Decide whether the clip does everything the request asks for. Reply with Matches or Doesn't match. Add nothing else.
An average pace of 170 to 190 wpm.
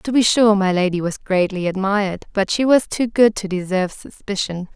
Doesn't match